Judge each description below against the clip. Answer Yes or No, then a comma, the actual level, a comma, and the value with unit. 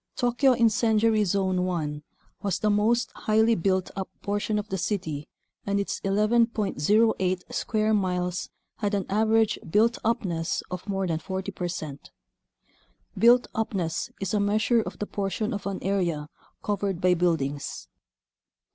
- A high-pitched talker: Yes, high, 200 Hz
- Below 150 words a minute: Yes, average, 140 wpm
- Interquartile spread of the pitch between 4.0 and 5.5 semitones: No, average, 3.3 semitones